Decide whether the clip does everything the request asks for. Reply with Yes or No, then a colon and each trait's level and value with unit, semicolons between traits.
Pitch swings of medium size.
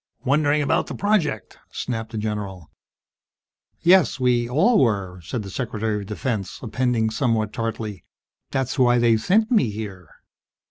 Yes: average, 4.0 semitones